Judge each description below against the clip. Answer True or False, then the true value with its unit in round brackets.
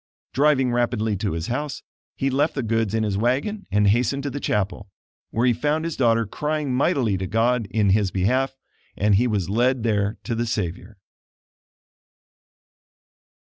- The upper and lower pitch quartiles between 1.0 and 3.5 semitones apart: False (4.3 semitones)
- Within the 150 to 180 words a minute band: True (165 wpm)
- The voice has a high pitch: False (115 Hz)